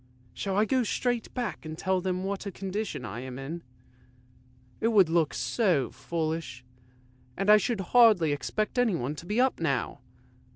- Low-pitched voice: No, high, 190 Hz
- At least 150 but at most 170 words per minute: Yes, average, 165 wpm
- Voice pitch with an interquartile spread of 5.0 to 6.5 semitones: Yes, average, 5.3 semitones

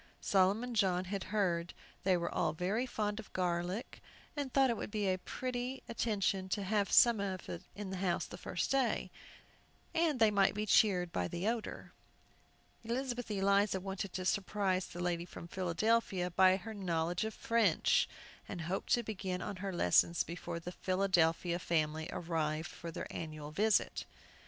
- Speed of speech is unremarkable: Yes, average, 160 wpm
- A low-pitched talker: No, high, 190 Hz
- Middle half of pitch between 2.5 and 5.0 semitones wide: Yes, average, 3.5 semitones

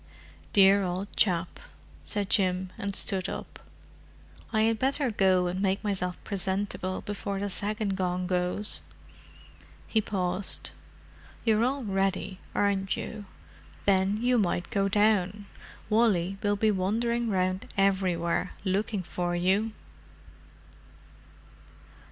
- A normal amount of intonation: No, narrow, 2.2 semitones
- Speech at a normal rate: No, slow, 115 wpm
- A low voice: No, high, 195 Hz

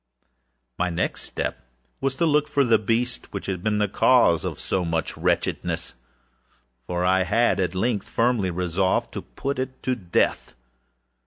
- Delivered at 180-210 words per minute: No, average, 165 wpm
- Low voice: Yes, low, 100 Hz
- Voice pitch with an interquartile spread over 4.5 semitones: Yes, wide, 5.5 semitones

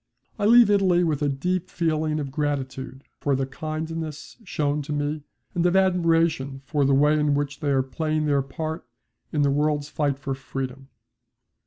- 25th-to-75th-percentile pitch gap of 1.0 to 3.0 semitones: Yes, average, 2.7 semitones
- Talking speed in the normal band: Yes, average, 175 wpm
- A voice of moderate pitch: Yes, medium, 150 Hz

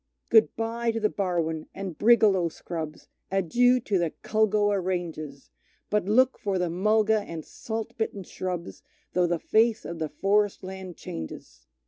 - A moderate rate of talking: Yes, average, 150 wpm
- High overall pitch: Yes, high, 195 Hz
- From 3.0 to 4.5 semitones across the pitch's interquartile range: Yes, average, 4.2 semitones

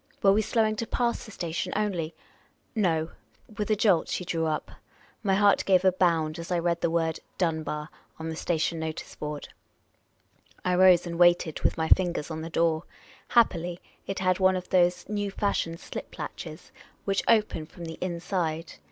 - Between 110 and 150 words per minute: No, average, 185 wpm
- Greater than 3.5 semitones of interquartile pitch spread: No, average, 2.9 semitones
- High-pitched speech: No, medium, 175 Hz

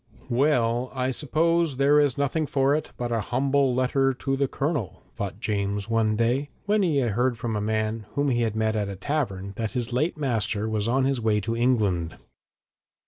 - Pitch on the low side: Yes, low, 125 Hz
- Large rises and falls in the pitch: No, average, 4.1 semitones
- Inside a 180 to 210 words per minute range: Yes, average, 190 wpm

